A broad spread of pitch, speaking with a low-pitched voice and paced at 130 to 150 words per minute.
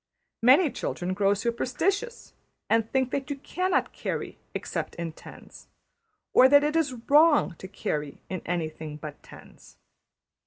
No: wide, 8.5 semitones; high, 245 Hz; average, 140 wpm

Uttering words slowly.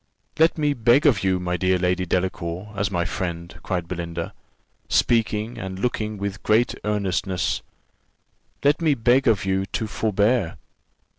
No: average, 145 wpm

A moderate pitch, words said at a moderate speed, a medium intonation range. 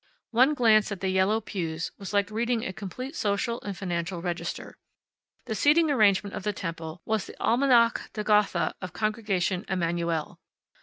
No: high, 200 Hz; average, 165 wpm; average, 4.0 semitones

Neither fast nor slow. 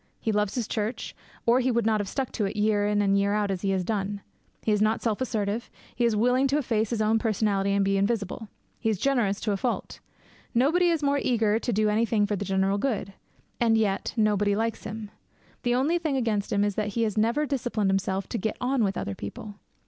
No: fast, 235 wpm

